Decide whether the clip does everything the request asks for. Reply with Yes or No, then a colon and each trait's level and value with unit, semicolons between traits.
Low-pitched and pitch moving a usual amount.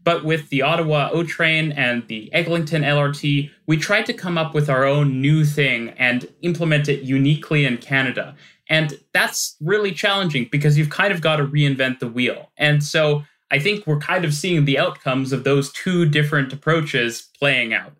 No: medium, 150 Hz; average, 3.0 semitones